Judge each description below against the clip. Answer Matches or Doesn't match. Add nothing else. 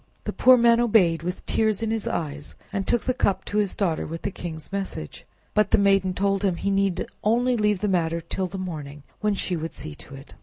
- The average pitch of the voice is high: Matches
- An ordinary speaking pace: Doesn't match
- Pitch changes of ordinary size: Matches